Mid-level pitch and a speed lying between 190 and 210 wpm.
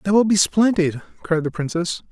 Yes: medium, 170 Hz; average, 200 wpm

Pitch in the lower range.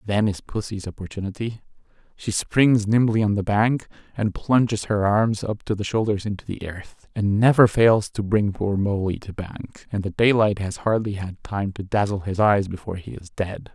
Yes: low, 105 Hz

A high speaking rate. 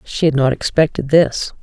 No: average, 185 wpm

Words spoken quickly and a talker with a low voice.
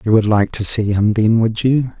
Yes: fast, 270 wpm; low, 110 Hz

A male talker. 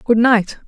No: female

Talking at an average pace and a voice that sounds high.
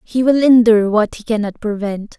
Yes: average, 190 wpm; high, 220 Hz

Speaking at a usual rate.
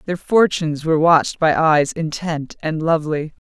Yes: average, 155 wpm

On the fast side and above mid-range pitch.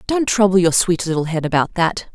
No: fast, 225 wpm; medium, 180 Hz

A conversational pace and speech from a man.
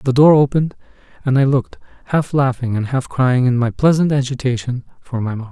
Yes: average, 195 wpm; male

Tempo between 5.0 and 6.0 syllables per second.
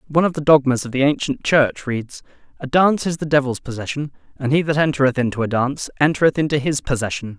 No: 6.4 syllables/s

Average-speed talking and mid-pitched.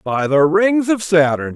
Yes: average, 195 wpm; medium, 170 Hz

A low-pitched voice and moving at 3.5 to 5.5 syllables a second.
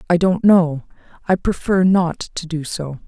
No: medium, 170 Hz; 4.2 syllables/s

